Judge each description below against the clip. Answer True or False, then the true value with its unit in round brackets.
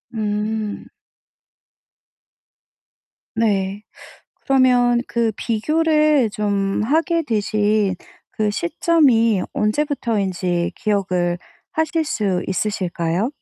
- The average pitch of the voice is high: True (215 Hz)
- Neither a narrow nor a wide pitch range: True (4.6 semitones)